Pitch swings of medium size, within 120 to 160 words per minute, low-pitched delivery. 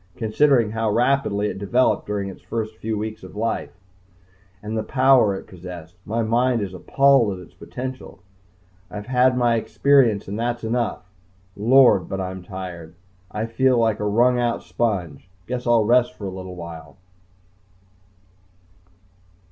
Yes: average, 4.1 semitones; average, 150 wpm; low, 110 Hz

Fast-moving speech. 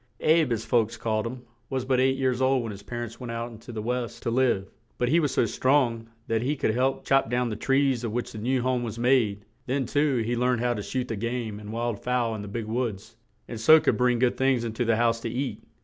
Yes: fast, 260 wpm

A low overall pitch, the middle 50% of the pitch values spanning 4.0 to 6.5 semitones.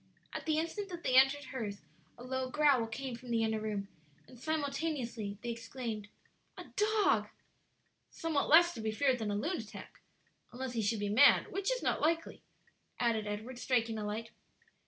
No: very high, 250 Hz; average, 5.1 semitones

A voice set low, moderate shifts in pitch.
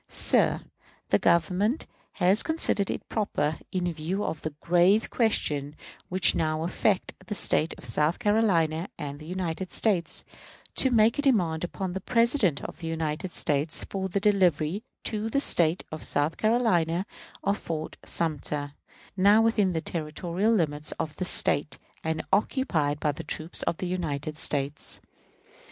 No: medium, 175 Hz; average, 4.6 semitones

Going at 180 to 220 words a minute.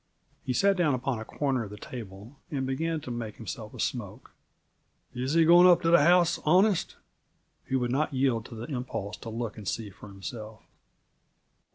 Yes: average, 190 wpm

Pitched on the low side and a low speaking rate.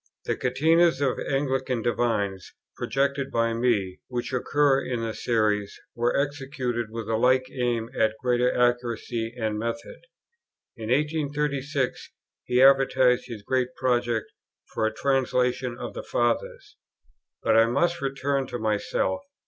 Yes: low, 125 Hz; slow, 130 wpm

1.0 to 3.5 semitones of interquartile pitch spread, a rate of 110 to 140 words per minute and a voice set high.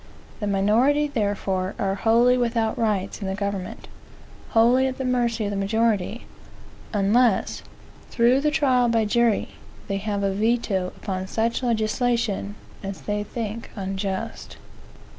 Yes: average, 3.2 semitones; slow, 135 wpm; high, 220 Hz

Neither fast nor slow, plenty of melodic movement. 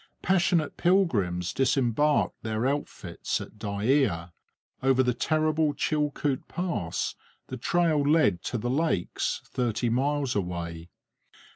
No: slow, 110 wpm; wide, 6.4 semitones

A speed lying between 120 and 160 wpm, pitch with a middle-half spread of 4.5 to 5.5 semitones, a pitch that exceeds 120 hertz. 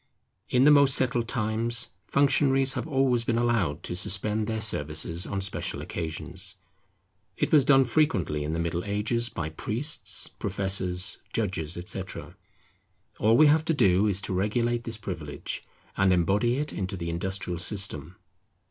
No: average, 150 wpm; average, 5.2 semitones; low, 105 Hz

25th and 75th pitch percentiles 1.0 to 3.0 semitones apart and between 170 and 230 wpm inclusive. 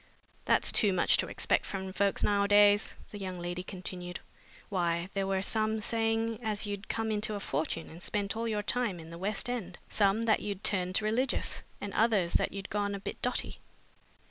Yes: narrow, 2.6 semitones; average, 190 wpm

